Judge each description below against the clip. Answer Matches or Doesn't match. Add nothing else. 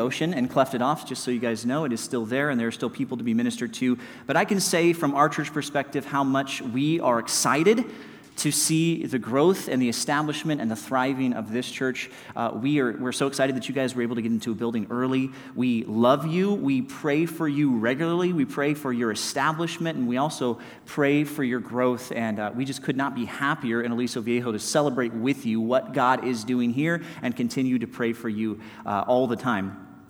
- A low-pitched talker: Matches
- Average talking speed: Doesn't match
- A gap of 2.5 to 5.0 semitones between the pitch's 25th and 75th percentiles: Matches